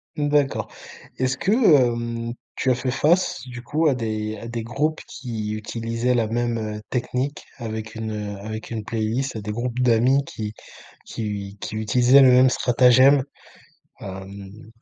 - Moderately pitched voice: No, low, 120 Hz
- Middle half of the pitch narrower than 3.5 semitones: Yes, average, 2.9 semitones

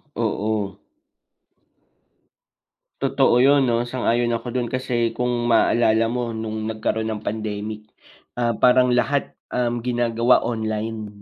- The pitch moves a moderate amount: No, narrow, 1.9 semitones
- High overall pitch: No, low, 115 Hz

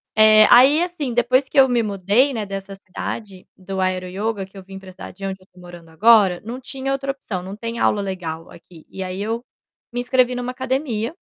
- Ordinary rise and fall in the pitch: Yes, average, 4.8 semitones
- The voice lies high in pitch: Yes, high, 215 Hz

